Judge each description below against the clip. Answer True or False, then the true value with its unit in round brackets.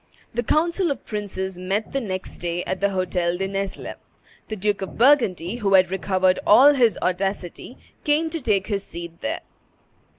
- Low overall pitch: False (195 Hz)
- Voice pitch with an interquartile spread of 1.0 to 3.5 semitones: False (4.2 semitones)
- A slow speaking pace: False (170 wpm)